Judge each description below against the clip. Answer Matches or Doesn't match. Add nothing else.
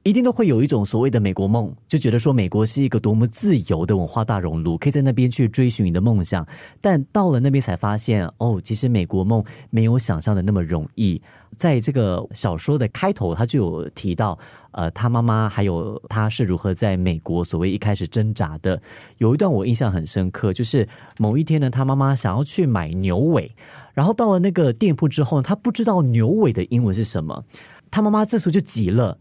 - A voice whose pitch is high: Doesn't match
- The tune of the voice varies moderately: Doesn't match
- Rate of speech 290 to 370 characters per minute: Matches